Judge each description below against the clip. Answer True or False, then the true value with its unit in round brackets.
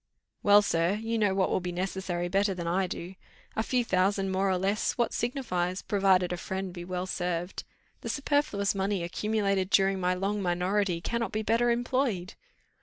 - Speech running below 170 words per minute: False (180 wpm)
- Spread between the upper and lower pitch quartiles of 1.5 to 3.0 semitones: True (2.5 semitones)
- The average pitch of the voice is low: False (195 Hz)